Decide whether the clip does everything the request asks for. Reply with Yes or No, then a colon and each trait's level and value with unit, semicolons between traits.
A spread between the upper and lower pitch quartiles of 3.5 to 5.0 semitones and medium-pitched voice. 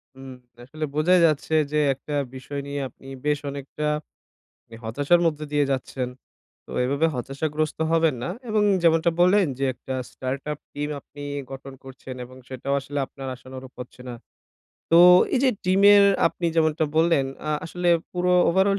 Yes: average, 3.8 semitones; medium, 150 Hz